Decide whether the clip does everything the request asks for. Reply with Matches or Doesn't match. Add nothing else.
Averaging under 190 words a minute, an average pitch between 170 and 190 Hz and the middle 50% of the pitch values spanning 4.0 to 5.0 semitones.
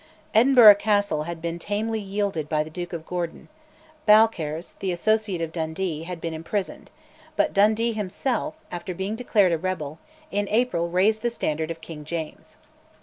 Matches